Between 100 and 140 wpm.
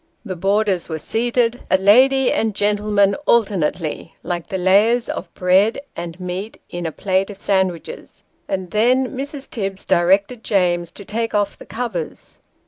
No: average, 150 wpm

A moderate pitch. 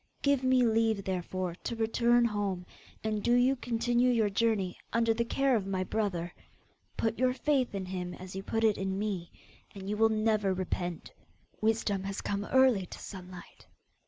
No: high, 215 Hz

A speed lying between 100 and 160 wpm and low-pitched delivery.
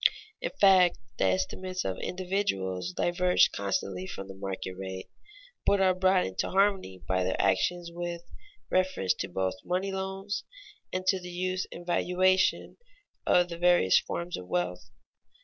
No: average, 150 wpm; medium, 175 Hz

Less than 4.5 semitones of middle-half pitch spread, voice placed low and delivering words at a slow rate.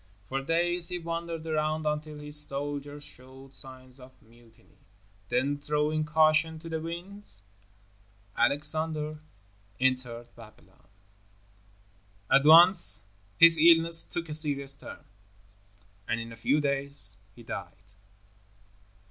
No: average, 3.7 semitones; medium, 150 Hz; slow, 115 wpm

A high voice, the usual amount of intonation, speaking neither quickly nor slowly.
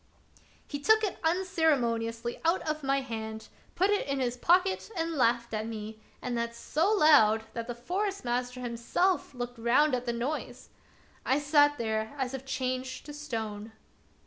Yes: very high, 255 Hz; average, 4.8 semitones; average, 165 wpm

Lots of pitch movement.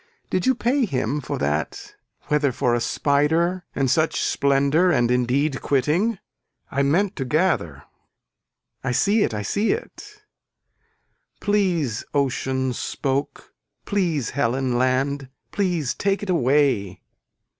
Yes: wide, 6.1 semitones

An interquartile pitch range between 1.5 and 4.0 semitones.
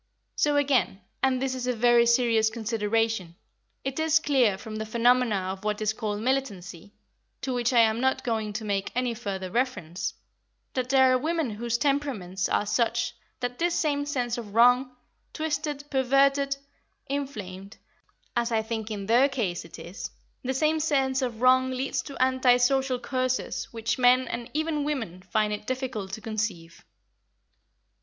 Yes: average, 3.6 semitones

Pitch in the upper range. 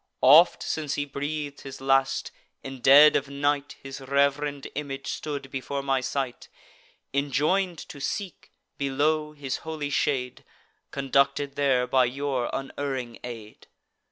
No: medium, 140 Hz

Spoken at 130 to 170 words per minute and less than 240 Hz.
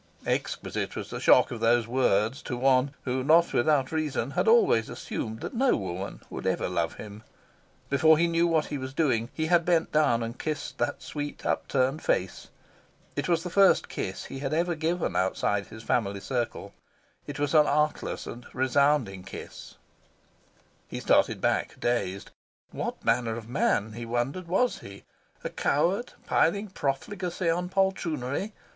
Yes: average, 165 wpm; medium, 140 Hz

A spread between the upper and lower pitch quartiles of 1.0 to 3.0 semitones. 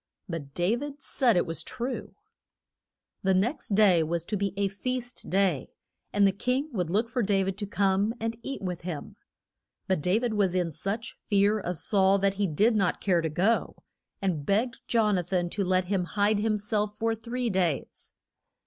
No: average, 3.7 semitones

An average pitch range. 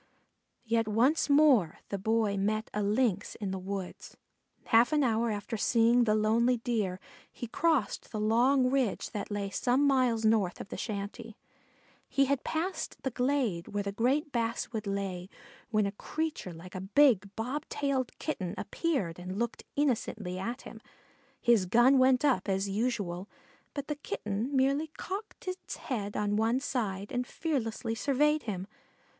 Yes: average, 4.6 semitones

